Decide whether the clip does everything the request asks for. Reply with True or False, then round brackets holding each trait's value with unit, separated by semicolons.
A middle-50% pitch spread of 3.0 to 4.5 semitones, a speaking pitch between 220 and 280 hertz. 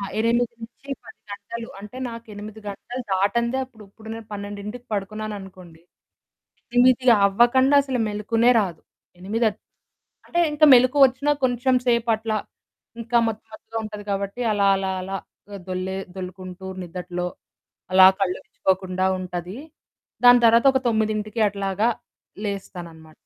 False (3.6 semitones; 210 Hz)